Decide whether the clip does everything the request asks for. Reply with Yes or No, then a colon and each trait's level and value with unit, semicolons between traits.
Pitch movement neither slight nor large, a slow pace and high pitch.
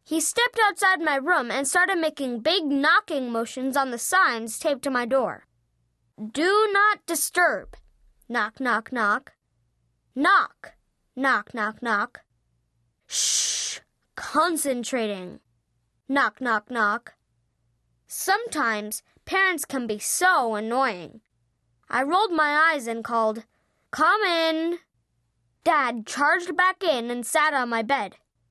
No: wide, 7.5 semitones; slow, 120 wpm; very high, 250 Hz